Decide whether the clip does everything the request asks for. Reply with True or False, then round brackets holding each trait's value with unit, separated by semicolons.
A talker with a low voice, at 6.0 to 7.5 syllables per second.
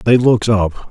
True (110 Hz; 6.5 syllables/s)